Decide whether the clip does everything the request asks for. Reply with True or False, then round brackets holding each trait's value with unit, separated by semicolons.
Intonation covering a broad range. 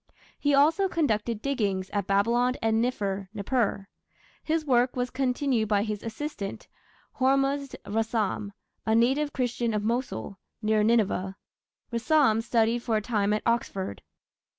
False (3.8 semitones)